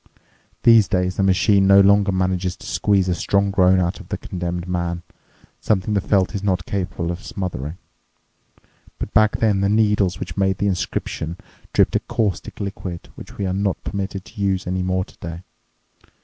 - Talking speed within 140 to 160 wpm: No, average, 175 wpm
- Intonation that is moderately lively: No, narrow, 1.6 semitones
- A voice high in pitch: No, very low, 95 Hz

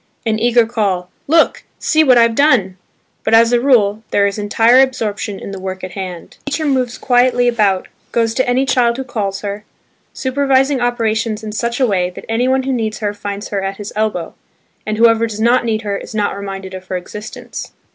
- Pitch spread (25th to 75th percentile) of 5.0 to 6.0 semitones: No, average, 3.5 semitones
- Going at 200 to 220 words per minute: Yes, fast, 205 wpm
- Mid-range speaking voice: No, high, 225 Hz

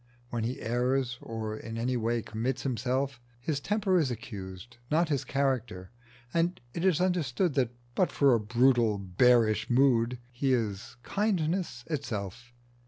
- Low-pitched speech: Yes, low, 125 Hz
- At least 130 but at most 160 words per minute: Yes, average, 145 wpm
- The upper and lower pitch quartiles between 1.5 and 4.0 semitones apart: Yes, average, 3.7 semitones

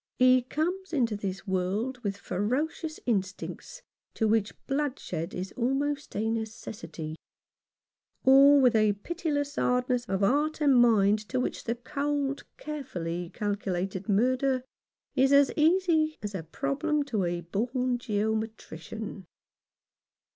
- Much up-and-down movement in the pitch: Yes, wide, 5.8 semitones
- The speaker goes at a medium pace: No, slow, 120 wpm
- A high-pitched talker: Yes, high, 245 Hz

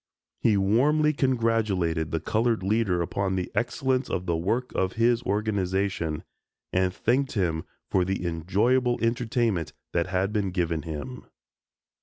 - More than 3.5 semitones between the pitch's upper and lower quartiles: Yes, average, 4.8 semitones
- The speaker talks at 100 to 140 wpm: Yes, slow, 135 wpm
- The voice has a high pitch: No, low, 100 Hz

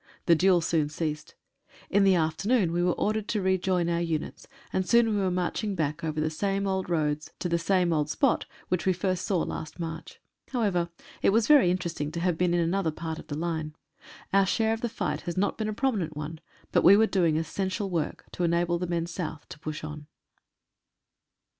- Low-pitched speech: No, medium, 175 Hz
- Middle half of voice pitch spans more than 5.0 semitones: No, average, 3.4 semitones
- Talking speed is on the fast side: Yes, fast, 210 wpm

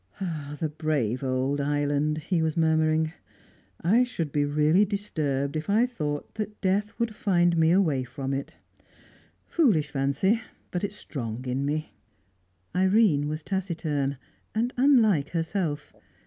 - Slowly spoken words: Yes, slow, 130 wpm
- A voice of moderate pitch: Yes, medium, 155 Hz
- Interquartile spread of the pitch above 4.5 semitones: Yes, average, 5.1 semitones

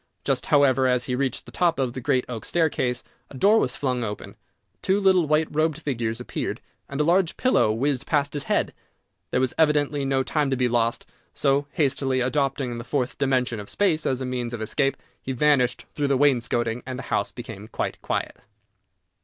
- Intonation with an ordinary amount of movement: Yes, average, 3.0 semitones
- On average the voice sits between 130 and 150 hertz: Yes, low, 135 Hz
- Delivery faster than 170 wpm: Yes, average, 195 wpm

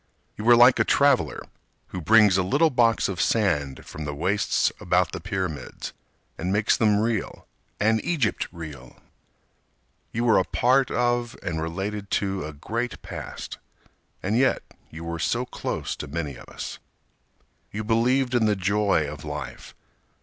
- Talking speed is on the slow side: No, average, 155 wpm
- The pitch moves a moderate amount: No, wide, 6.0 semitones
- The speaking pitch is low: Yes, low, 105 Hz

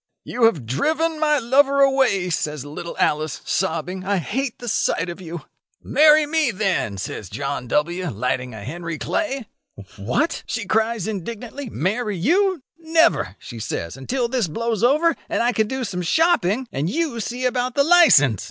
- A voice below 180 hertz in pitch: No, high, 220 Hz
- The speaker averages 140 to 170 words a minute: Yes, average, 165 wpm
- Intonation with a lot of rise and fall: Yes, wide, 8.8 semitones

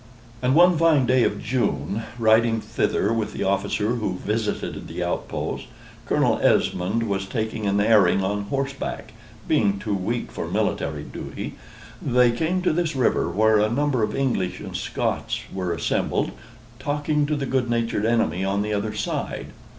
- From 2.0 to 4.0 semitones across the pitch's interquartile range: No, average, 4.4 semitones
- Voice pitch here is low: Yes, low, 115 Hz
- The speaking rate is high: No, average, 160 wpm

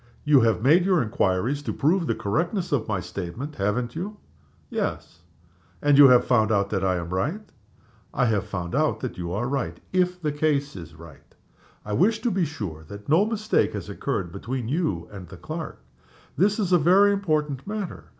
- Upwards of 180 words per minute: Yes, average, 190 wpm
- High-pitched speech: No, low, 135 Hz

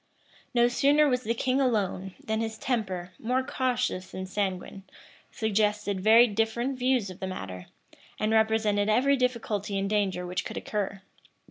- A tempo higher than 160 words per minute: No, average, 150 wpm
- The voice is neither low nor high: No, high, 220 Hz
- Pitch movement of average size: Yes, average, 4.0 semitones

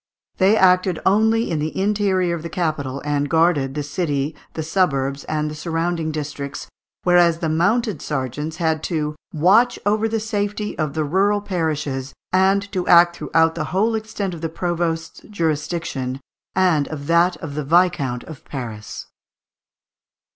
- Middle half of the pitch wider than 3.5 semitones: Yes, average, 3.9 semitones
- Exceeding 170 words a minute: No, average, 155 wpm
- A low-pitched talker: No, medium, 165 Hz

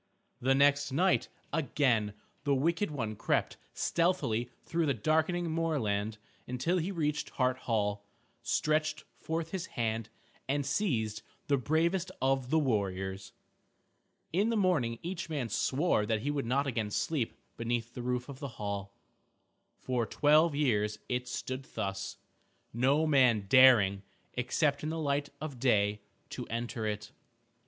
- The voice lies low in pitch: Yes, low, 130 Hz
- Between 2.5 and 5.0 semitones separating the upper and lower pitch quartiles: No, wide, 5.6 semitones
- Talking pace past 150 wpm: No, average, 140 wpm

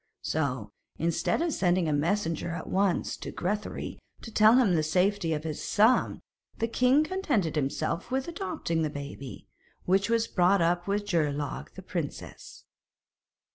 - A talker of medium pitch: Yes, medium, 180 Hz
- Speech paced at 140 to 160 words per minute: Yes, average, 155 wpm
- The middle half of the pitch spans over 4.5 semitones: Yes, wide, 5.6 semitones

